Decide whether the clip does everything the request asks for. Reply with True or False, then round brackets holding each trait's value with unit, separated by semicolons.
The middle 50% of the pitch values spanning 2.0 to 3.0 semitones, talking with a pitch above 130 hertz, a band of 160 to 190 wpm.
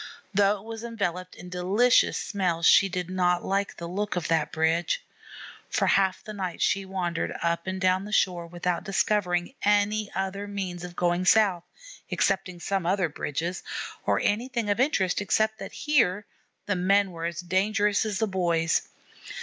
True (2.6 semitones; 190 Hz; 165 wpm)